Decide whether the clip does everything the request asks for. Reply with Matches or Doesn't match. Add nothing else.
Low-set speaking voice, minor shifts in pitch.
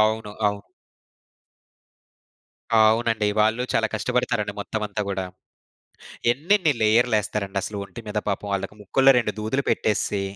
Matches